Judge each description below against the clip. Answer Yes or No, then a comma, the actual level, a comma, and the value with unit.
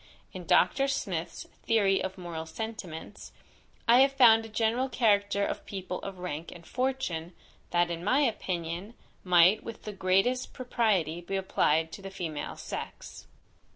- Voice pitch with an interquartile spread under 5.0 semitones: Yes, average, 4.6 semitones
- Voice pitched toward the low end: No, high, 195 Hz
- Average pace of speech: Yes, average, 150 wpm